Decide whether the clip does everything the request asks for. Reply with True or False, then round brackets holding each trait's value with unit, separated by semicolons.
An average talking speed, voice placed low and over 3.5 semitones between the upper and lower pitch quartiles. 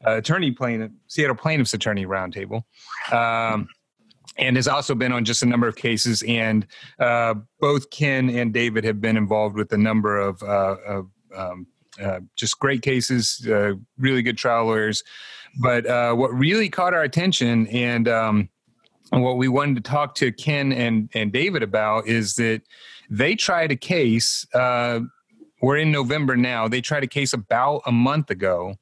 False (175 wpm; 120 Hz; 3.1 semitones)